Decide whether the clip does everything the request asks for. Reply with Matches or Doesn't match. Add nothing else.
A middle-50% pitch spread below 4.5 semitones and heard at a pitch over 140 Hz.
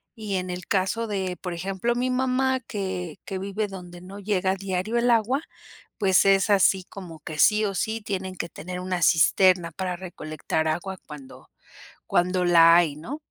Matches